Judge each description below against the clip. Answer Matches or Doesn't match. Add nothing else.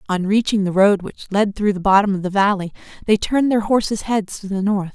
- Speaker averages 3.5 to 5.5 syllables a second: Doesn't match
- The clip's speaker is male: Doesn't match